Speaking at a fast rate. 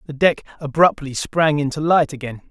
No: average, 165 wpm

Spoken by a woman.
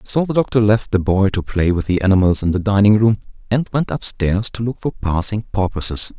No: male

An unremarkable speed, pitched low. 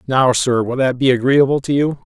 No: fast, 230 wpm; low, 130 Hz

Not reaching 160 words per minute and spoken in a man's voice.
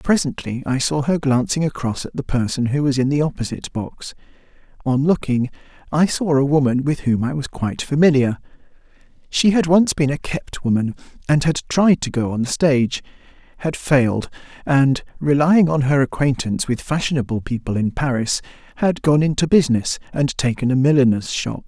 No: average, 175 wpm; male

